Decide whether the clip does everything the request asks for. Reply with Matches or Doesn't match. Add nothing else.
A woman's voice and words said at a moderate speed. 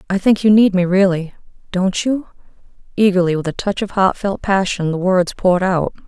Matches